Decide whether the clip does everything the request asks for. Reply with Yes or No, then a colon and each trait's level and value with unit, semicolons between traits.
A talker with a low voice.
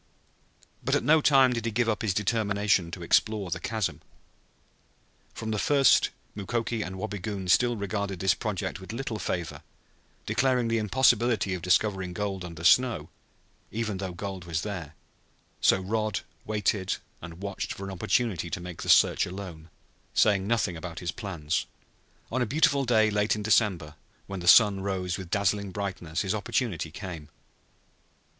Yes: low, 100 Hz